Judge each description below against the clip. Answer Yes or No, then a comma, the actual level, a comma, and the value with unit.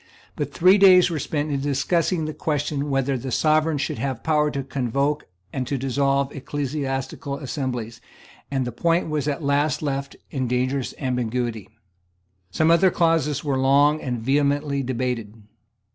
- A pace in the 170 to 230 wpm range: No, average, 150 wpm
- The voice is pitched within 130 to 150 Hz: Yes, medium, 140 Hz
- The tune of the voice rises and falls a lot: No, narrow, 2.5 semitones